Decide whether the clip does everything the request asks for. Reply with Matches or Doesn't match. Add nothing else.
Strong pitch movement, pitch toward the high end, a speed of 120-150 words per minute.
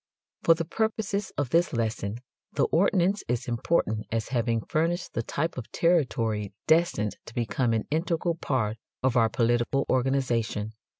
Doesn't match